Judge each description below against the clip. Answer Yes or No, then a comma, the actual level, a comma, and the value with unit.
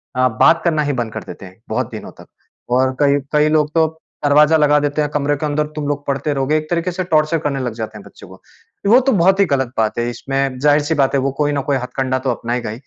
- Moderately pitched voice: Yes, medium, 145 Hz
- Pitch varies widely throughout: No, average, 2.8 semitones